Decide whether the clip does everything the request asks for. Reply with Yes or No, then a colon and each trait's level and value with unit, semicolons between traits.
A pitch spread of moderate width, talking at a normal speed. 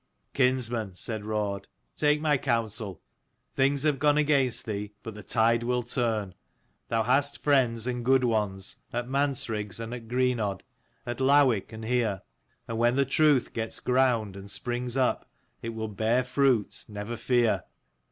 Yes: average, 3.1 semitones; average, 160 wpm